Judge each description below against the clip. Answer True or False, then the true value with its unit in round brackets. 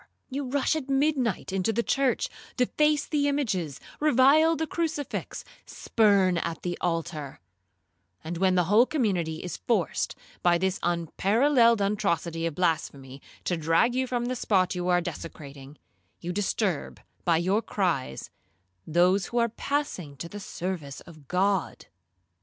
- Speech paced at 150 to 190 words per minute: False (140 wpm)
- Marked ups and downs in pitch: True (6.7 semitones)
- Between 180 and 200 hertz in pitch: True (190 Hz)